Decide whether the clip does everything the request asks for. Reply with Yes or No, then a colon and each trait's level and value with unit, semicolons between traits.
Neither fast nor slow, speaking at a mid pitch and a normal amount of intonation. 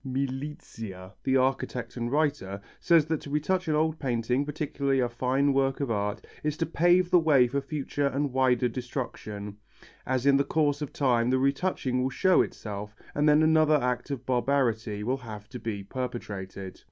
No: average, 175 wpm; low, 130 Hz; average, 3.7 semitones